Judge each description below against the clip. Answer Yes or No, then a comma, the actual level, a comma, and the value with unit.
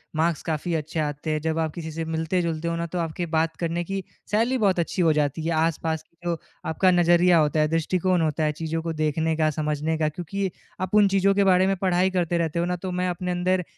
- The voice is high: No, medium, 165 Hz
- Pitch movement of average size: No, narrow, 2.2 semitones